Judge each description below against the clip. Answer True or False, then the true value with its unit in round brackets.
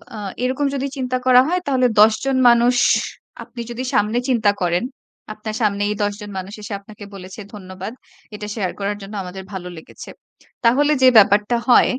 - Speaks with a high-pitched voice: True (215 Hz)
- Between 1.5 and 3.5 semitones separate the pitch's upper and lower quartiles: False (4.0 semitones)